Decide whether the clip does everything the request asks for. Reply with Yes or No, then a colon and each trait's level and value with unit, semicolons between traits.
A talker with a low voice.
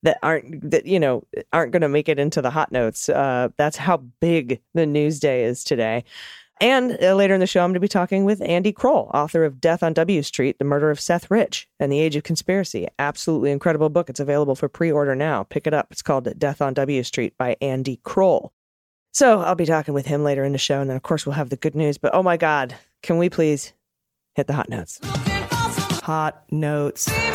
No: medium, 155 Hz